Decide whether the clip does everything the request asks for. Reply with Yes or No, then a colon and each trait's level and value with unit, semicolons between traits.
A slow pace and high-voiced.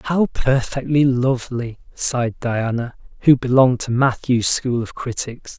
No: slow, 130 wpm; low, 125 Hz